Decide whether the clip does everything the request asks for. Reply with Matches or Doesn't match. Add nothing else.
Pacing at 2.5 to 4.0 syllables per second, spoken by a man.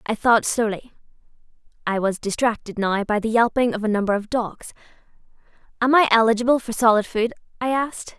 Doesn't match